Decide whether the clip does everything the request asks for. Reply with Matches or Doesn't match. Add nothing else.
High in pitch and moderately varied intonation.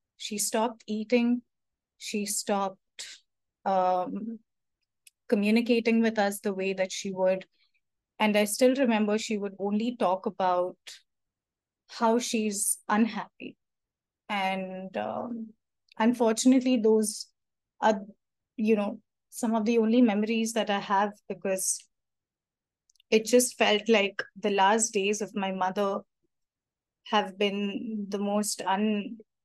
Doesn't match